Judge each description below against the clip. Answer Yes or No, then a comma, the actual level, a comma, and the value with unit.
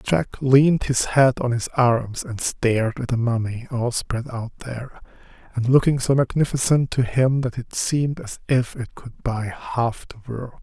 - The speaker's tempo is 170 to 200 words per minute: Yes, average, 185 wpm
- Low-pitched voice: Yes, low, 125 Hz